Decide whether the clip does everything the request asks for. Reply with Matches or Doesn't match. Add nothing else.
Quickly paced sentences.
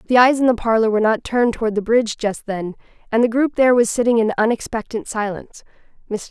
Matches